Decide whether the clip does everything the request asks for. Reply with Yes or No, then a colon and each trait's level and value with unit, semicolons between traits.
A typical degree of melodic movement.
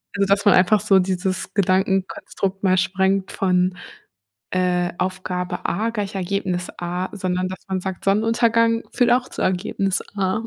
No: narrow, 1.6 semitones